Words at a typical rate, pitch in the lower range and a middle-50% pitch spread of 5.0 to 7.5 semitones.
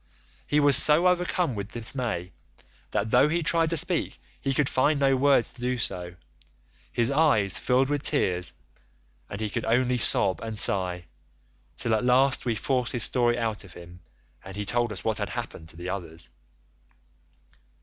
Yes: average, 175 wpm; low, 120 Hz; wide, 5.4 semitones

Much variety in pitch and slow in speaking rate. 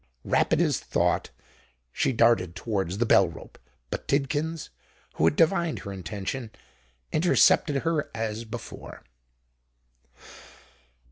Yes: wide, 7.2 semitones; slow, 110 wpm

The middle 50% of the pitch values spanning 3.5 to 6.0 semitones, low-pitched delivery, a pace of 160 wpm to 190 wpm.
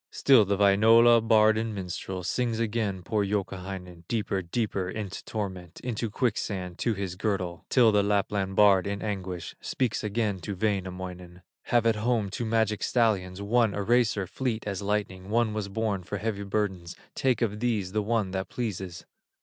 No: average, 2.9 semitones; low, 105 Hz; average, 165 wpm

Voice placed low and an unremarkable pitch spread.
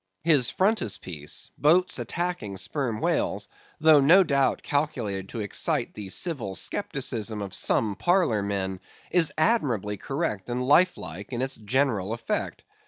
No: low, 120 Hz; wide, 7.5 semitones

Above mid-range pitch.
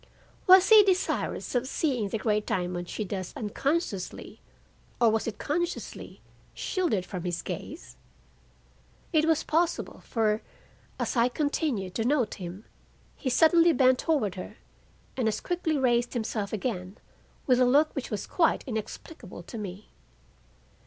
Yes: high, 240 Hz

